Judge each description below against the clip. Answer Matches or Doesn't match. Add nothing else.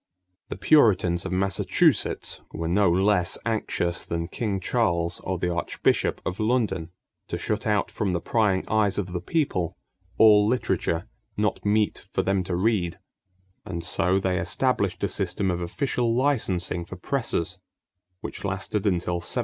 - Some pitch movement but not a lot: Matches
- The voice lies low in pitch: Matches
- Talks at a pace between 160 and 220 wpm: Doesn't match